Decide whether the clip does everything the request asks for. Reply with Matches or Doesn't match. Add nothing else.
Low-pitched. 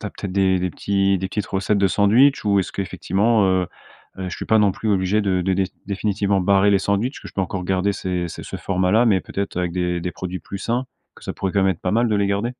Matches